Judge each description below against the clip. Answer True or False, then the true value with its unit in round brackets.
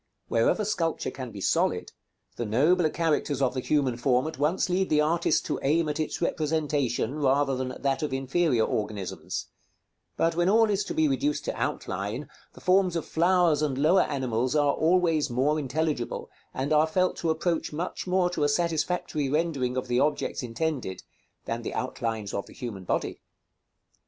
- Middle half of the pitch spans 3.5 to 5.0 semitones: True (4.4 semitones)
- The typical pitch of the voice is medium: True (150 Hz)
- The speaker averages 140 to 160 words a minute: False (175 wpm)